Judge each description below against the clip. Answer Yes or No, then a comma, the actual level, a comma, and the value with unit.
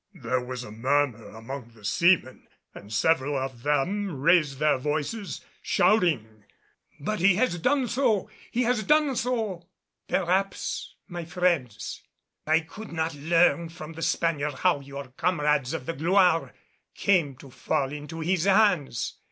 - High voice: No, medium, 160 Hz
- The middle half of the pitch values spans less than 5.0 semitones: No, average, 5.3 semitones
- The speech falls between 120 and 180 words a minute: Yes, average, 145 wpm